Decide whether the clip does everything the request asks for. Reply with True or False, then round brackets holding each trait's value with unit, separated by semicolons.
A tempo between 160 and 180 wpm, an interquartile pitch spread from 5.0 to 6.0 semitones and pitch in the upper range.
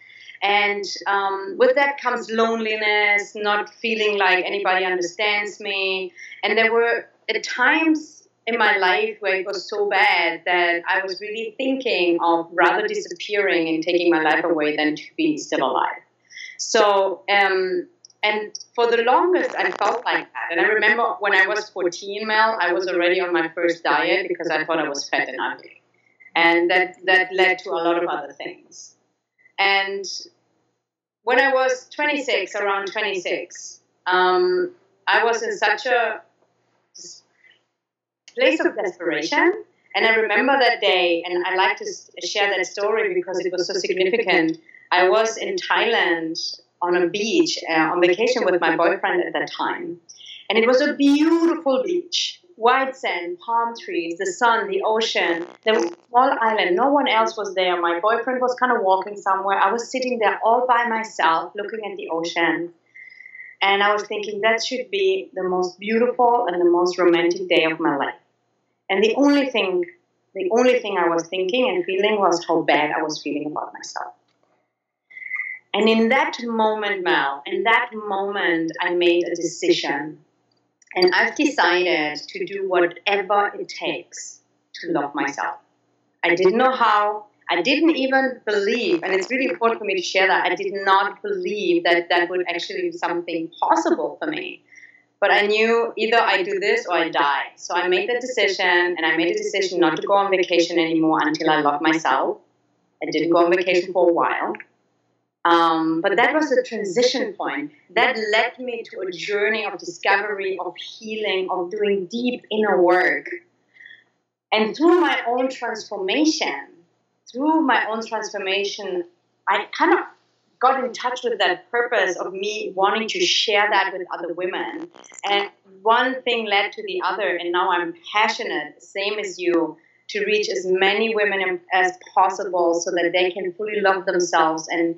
True (170 wpm; 5.4 semitones; 200 Hz)